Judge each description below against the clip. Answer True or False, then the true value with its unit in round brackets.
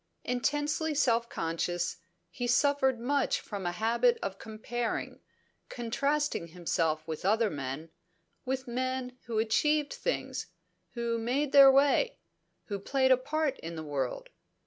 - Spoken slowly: True (130 wpm)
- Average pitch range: False (6.0 semitones)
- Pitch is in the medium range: False (240 Hz)